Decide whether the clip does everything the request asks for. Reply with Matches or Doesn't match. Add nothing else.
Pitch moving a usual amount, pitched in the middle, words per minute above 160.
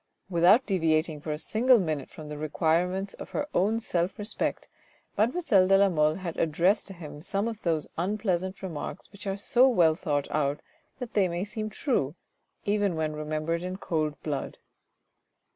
Matches